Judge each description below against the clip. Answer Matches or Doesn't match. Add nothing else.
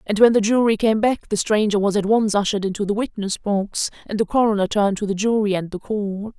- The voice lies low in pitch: Doesn't match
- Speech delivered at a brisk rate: Matches